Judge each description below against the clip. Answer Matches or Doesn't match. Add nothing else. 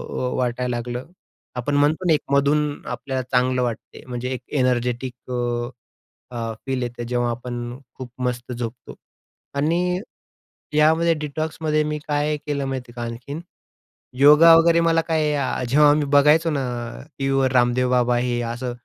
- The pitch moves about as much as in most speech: Matches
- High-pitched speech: Doesn't match